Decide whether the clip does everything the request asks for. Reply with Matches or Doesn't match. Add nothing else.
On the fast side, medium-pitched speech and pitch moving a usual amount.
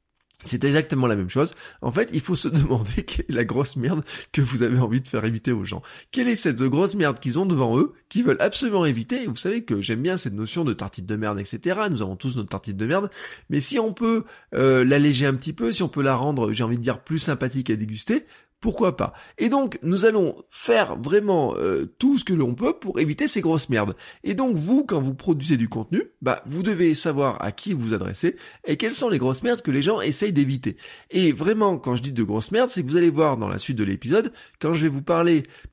Doesn't match